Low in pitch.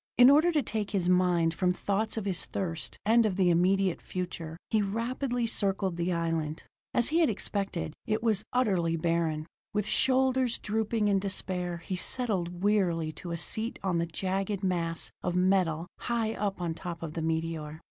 No: high, 190 Hz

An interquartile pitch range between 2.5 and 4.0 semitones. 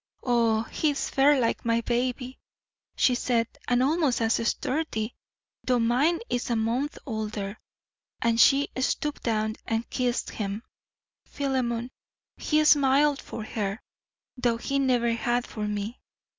Yes: average, 3.0 semitones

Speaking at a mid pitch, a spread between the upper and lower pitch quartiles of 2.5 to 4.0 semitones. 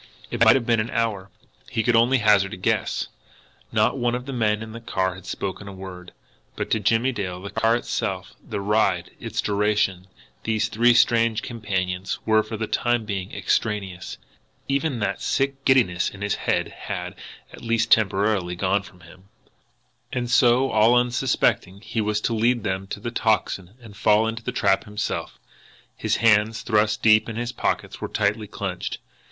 No: low, 110 Hz; average, 3.0 semitones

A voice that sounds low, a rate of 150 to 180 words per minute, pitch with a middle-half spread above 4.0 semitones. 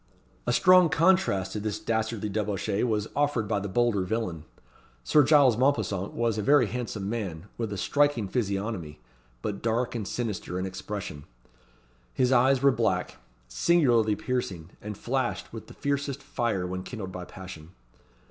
Yes: low, 110 Hz; average, 155 wpm; average, 4.5 semitones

